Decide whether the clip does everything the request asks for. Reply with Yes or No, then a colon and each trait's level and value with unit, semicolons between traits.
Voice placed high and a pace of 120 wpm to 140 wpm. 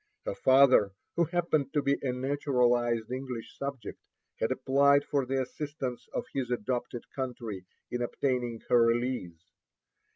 No: low, 130 Hz; slow, 135 wpm